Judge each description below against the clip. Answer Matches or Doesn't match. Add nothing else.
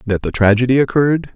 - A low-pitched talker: Matches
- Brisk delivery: Doesn't match